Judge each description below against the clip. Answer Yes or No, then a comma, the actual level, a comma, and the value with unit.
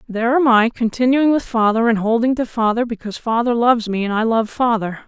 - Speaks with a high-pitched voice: Yes, high, 230 Hz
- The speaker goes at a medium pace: No, fast, 215 wpm